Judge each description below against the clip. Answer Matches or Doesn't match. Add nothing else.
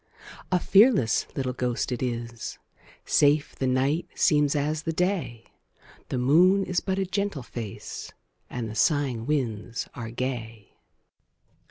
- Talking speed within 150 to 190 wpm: Doesn't match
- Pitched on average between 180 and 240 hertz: Doesn't match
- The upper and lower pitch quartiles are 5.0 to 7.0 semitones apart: Matches